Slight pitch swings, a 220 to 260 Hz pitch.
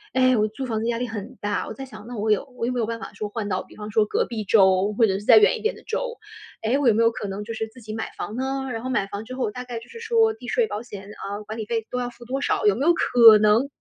No: average, 3.3 semitones; high, 230 Hz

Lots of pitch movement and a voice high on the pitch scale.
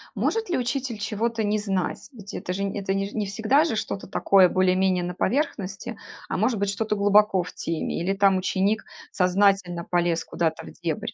No: average, 2.7 semitones; high, 195 Hz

